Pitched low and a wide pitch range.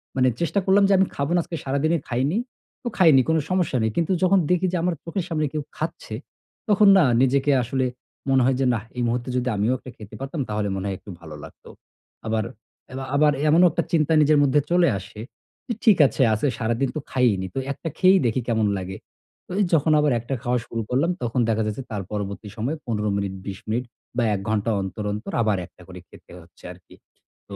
Yes: low, 130 Hz; wide, 6.8 semitones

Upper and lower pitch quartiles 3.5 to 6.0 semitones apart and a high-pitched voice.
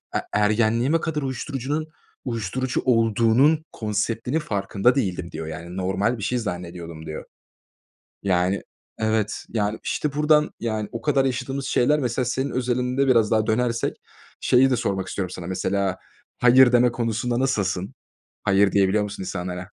No: average, 4.7 semitones; low, 115 Hz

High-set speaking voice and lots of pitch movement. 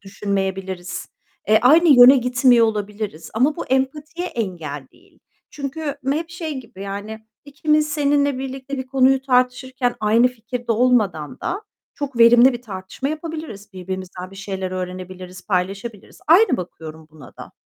Yes: high, 235 Hz; wide, 6.1 semitones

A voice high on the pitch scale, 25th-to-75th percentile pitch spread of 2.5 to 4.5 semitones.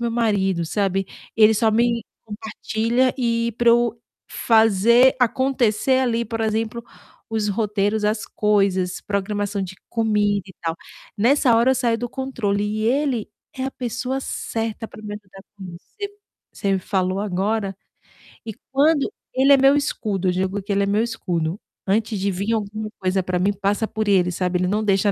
Yes: high, 215 Hz; average, 3.0 semitones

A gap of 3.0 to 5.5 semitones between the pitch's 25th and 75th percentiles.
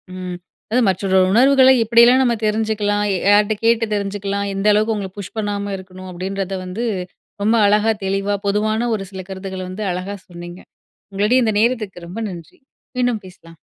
No: narrow, 2.6 semitones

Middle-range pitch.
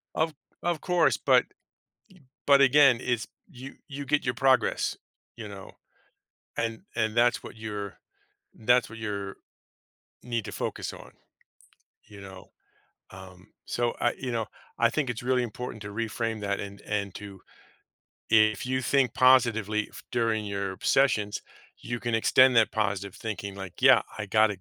No: low, 115 Hz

